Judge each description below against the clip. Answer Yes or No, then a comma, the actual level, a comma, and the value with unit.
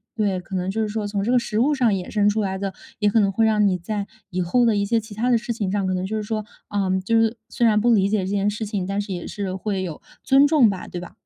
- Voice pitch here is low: No, high, 205 Hz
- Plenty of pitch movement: No, average, 2.7 semitones